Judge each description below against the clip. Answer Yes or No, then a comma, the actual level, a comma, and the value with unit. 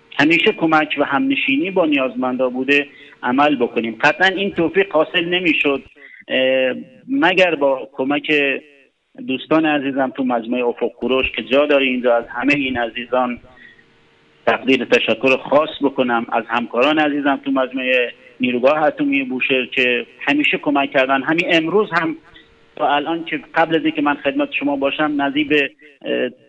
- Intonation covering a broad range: No, average, 3.4 semitones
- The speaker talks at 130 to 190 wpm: Yes, average, 140 wpm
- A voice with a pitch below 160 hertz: Yes, medium, 140 Hz